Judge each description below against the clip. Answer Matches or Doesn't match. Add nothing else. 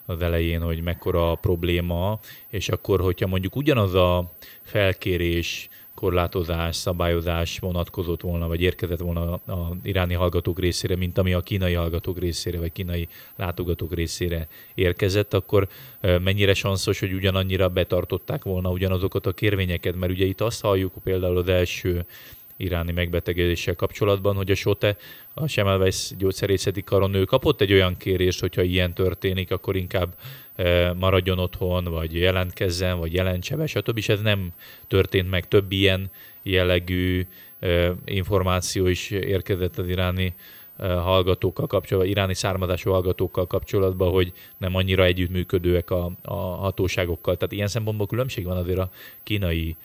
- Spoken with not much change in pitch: Matches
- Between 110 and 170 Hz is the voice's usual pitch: Doesn't match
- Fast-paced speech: Doesn't match